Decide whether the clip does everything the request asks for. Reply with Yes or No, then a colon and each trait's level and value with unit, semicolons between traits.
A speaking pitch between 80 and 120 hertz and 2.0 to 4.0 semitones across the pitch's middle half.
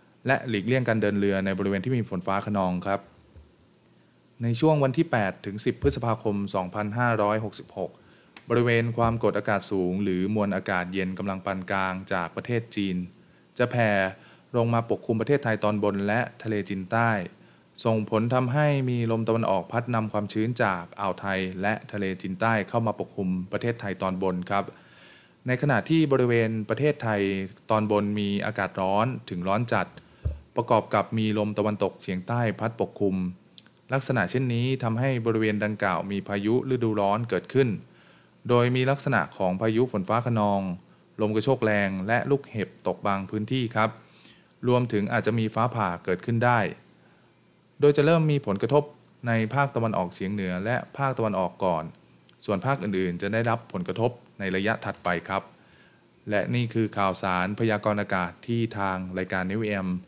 Yes: low, 105 Hz; average, 3.3 semitones